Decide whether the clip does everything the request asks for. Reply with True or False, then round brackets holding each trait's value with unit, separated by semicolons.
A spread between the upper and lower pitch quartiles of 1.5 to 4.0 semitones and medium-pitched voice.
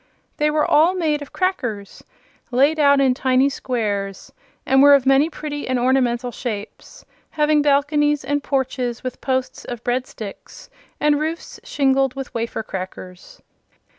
False (3.2 semitones; 270 Hz)